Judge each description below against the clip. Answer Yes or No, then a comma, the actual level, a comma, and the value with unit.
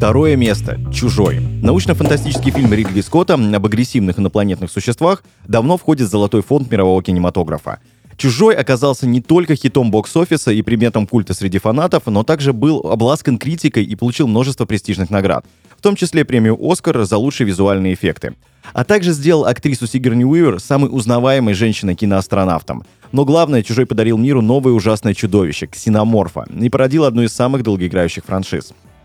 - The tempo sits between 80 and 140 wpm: No, average, 150 wpm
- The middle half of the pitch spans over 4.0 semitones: Yes, average, 5.1 semitones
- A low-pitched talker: Yes, low, 120 Hz